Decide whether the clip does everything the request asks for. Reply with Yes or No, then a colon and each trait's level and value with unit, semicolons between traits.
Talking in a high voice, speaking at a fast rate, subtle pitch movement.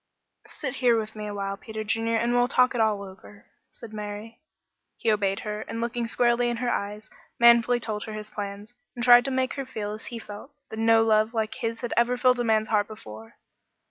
Yes: high, 225 Hz; fast, 215 wpm; narrow, 2.3 semitones